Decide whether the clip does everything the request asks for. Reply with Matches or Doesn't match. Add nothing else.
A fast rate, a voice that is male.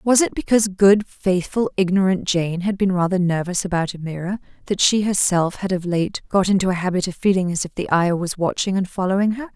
Doesn't match